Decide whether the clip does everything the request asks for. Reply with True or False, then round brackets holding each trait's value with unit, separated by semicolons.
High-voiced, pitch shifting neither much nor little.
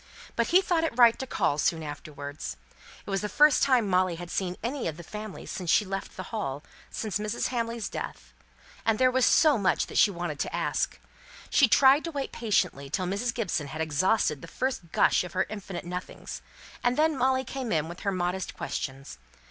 False (200 Hz; 6.3 semitones)